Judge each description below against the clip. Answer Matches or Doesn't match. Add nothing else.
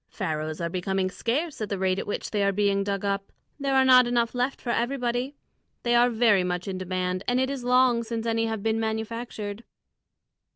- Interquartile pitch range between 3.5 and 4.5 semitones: Matches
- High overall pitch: Matches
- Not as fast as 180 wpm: Doesn't match